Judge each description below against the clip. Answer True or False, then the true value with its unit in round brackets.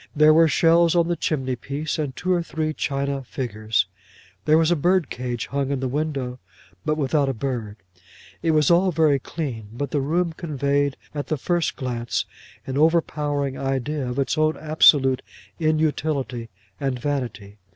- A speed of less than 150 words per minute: False (160 wpm)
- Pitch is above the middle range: False (145 Hz)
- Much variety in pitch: False (3.1 semitones)